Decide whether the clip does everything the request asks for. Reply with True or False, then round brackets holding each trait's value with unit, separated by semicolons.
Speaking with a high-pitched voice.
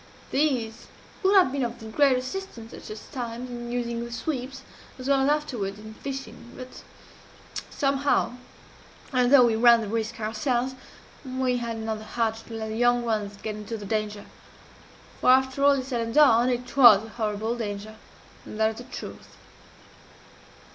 True (240 Hz)